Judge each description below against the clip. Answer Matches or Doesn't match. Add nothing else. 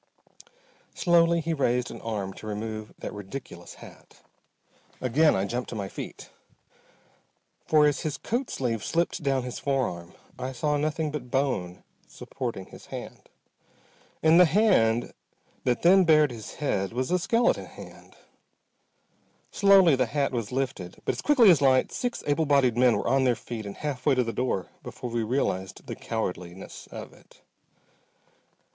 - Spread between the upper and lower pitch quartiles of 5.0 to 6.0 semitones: Matches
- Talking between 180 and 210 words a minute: Doesn't match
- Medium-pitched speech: Doesn't match